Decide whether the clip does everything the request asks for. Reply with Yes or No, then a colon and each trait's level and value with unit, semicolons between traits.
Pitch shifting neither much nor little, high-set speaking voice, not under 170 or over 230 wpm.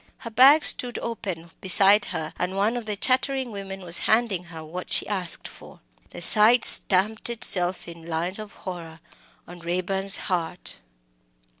No: average, 3.9 semitones; high, 195 Hz; average, 155 wpm